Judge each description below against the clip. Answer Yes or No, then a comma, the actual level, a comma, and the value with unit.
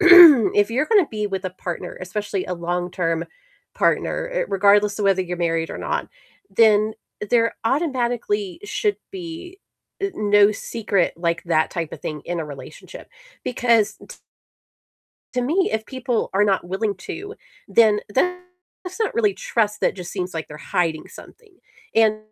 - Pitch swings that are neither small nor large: No, wide, 6.4 semitones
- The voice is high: Yes, high, 210 Hz